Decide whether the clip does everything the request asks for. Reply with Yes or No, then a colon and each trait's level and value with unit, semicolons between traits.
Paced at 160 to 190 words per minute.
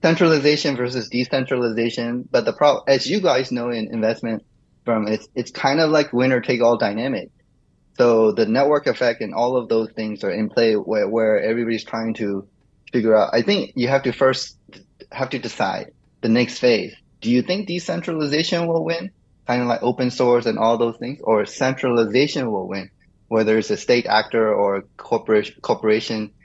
Yes: average, 180 wpm